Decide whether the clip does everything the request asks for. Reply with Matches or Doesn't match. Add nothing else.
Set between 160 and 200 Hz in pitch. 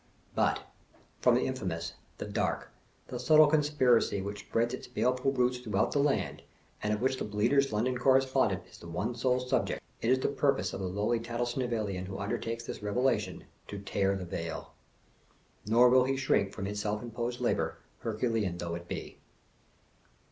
Doesn't match